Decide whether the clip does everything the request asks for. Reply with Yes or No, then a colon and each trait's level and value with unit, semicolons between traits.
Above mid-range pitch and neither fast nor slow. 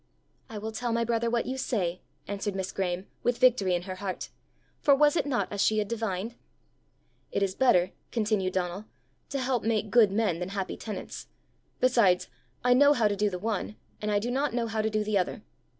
No: high, 215 Hz; fast, 210 wpm